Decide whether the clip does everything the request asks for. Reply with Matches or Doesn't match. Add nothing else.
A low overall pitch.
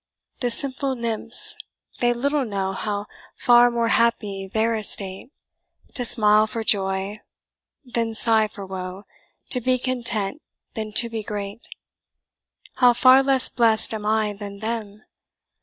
Doesn't match